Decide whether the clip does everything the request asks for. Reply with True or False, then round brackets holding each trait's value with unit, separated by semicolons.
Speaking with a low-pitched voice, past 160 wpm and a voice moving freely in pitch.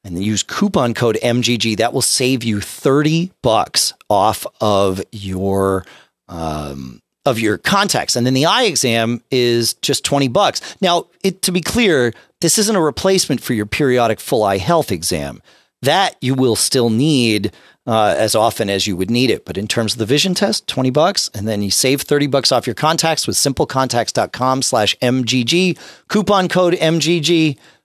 True (125 Hz; 175 wpm; 6.4 semitones)